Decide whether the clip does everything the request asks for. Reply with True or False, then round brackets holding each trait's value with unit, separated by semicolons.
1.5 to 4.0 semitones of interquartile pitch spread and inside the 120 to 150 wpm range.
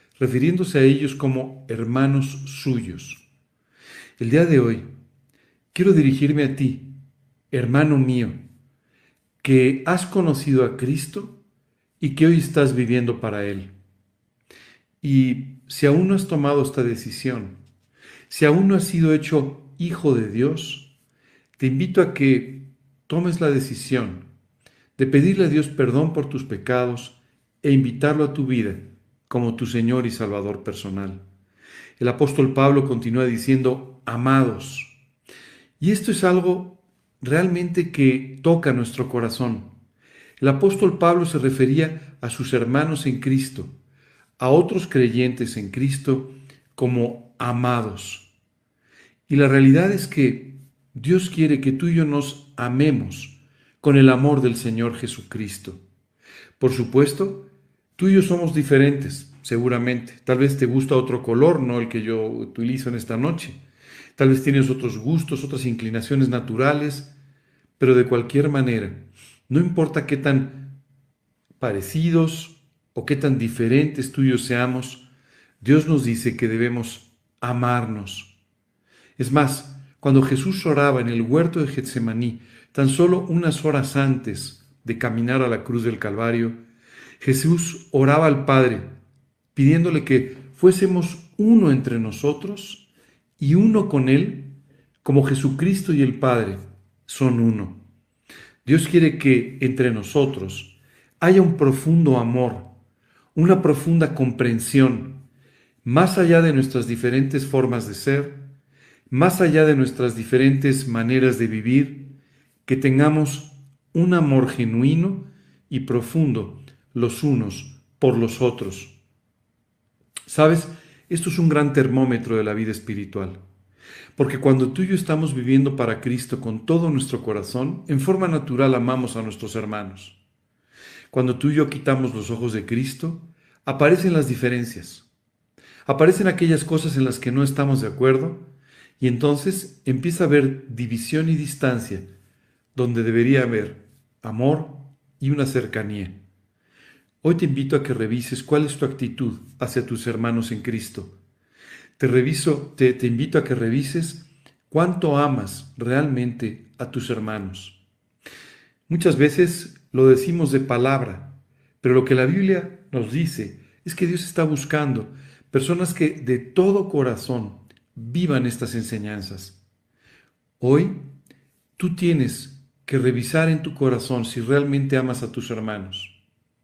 True (3.2 semitones; 135 wpm)